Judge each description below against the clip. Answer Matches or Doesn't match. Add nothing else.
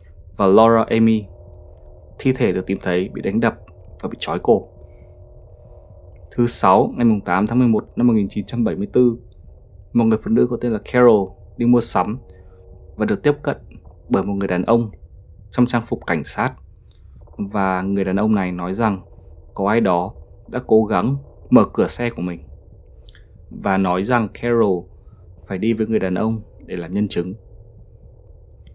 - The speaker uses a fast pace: Doesn't match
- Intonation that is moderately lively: Matches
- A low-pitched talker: Matches